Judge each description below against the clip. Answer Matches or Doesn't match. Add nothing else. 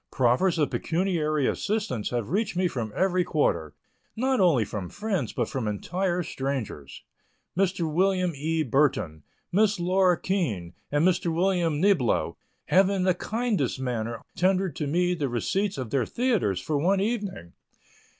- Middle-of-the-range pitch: Matches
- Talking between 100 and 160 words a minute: Matches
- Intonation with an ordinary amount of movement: Doesn't match